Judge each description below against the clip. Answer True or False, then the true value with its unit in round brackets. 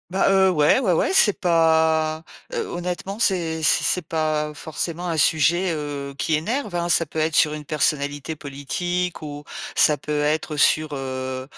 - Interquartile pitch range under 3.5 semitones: True (2.9 semitones)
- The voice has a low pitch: False (160 Hz)